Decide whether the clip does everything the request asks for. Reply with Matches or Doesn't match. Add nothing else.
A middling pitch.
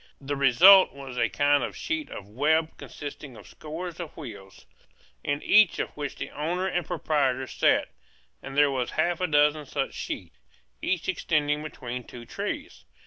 Matches